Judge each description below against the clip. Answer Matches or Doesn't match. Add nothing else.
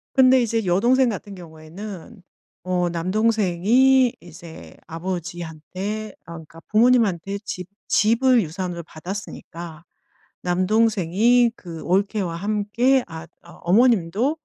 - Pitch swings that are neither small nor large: Matches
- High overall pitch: Matches